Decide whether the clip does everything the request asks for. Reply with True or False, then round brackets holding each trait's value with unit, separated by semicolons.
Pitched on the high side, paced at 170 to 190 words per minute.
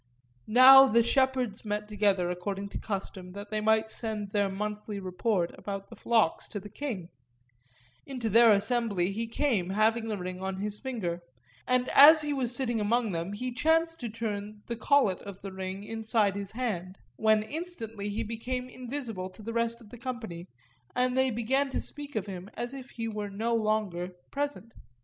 True (220 Hz; 180 wpm)